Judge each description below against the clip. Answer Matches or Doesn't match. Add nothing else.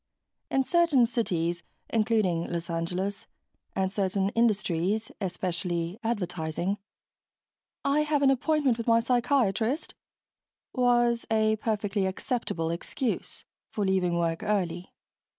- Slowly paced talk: Matches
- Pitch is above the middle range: Matches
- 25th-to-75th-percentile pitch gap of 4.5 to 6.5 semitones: Matches